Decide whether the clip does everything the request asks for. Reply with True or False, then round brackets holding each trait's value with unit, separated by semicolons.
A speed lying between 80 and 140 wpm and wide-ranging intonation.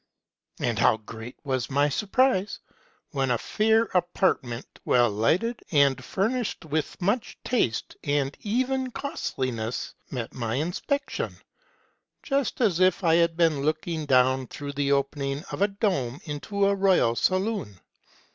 True (135 wpm; 7.3 semitones)